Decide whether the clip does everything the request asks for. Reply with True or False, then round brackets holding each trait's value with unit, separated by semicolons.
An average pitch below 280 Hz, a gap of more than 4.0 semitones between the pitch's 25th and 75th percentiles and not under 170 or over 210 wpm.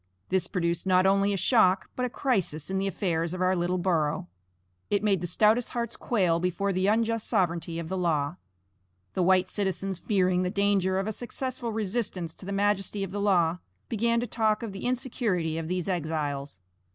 False (190 Hz; 3.2 semitones; 190 wpm)